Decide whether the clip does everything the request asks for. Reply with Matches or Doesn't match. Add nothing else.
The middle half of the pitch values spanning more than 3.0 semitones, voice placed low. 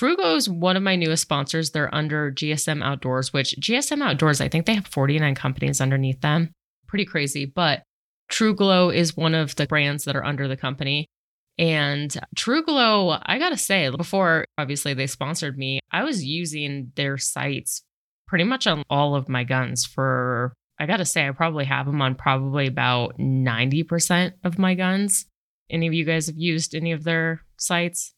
Doesn't match